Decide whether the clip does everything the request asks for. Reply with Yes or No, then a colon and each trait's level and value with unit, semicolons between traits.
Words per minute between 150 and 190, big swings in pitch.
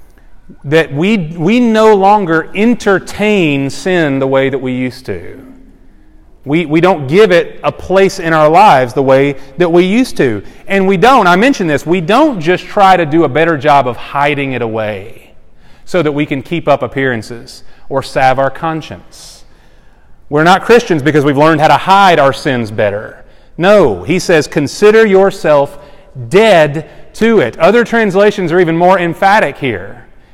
Yes: average, 170 wpm; wide, 5.9 semitones